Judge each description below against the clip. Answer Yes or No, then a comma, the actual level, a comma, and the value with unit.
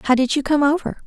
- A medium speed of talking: No, fast, 280 wpm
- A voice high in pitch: Yes, very high, 280 Hz